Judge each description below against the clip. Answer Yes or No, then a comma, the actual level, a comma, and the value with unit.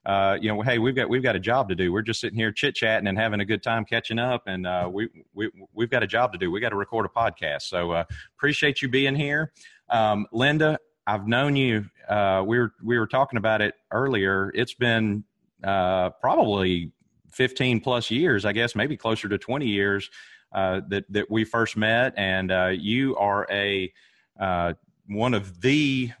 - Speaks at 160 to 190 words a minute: No, fast, 205 wpm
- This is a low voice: Yes, low, 110 Hz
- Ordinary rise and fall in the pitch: Yes, average, 3.7 semitones